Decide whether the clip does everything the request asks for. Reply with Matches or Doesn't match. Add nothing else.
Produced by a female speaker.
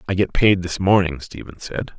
Doesn't match